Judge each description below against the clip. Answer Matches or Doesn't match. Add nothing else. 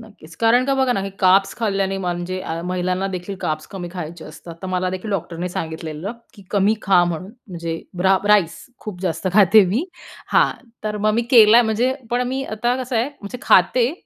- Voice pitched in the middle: Doesn't match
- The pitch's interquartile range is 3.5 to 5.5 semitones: Matches